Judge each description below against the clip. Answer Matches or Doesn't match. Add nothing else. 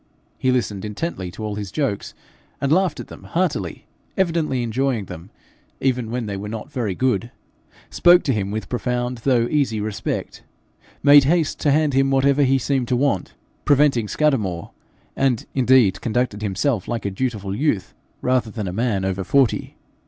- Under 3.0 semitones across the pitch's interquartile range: Doesn't match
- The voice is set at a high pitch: Doesn't match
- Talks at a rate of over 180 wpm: Doesn't match